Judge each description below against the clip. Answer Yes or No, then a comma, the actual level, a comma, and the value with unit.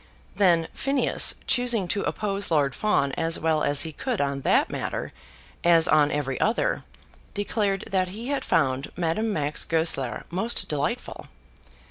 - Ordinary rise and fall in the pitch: No, wide, 6.0 semitones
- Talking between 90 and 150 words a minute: Yes, average, 145 wpm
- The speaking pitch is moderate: Yes, medium, 170 Hz